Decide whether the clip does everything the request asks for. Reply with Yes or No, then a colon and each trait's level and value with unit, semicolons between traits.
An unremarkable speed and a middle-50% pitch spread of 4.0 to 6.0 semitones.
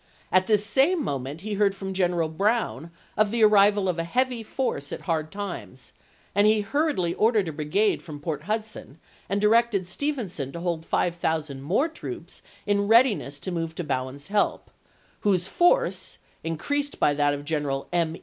Yes: average, 175 wpm; average, 5.3 semitones